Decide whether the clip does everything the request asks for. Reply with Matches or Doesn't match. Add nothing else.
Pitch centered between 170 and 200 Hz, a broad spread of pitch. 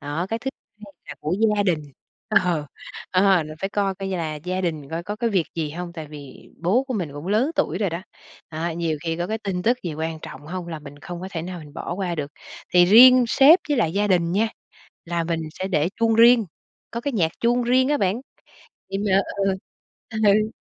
Doesn't match